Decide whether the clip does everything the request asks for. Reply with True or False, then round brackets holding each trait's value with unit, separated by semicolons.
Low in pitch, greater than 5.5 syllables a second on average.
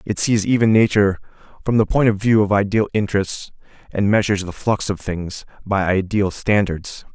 False (100 Hz; 5.3 syllables/s)